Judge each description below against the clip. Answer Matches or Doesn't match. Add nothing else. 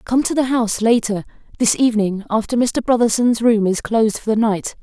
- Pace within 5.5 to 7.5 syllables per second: Matches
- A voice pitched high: Matches